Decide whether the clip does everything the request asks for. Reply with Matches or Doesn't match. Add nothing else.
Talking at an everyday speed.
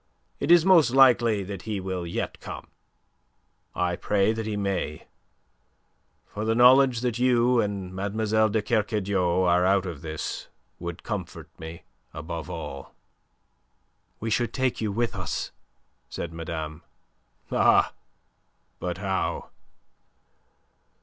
Doesn't match